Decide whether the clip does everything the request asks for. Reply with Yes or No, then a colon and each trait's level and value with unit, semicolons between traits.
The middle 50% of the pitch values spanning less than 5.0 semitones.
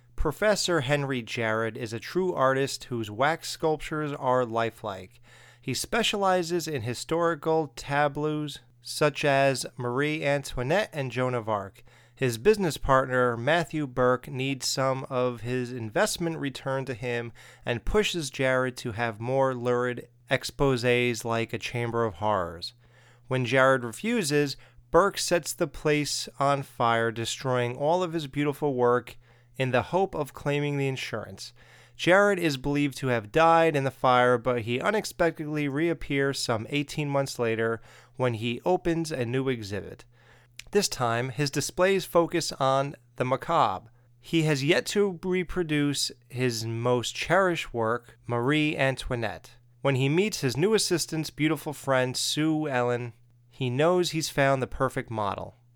Yes: average, 4.1 semitones